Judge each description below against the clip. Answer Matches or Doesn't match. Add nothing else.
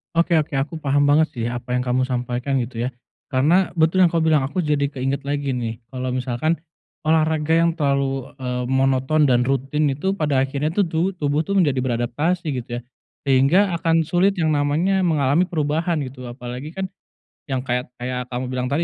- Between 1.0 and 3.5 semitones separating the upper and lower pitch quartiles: Doesn't match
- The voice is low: Doesn't match